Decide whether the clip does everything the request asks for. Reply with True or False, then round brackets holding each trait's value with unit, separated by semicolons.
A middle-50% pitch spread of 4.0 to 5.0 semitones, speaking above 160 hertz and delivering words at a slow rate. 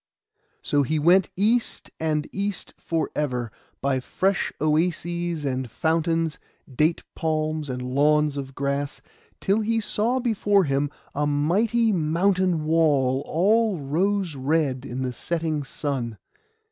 False (4.7 semitones; 155 Hz; 125 wpm)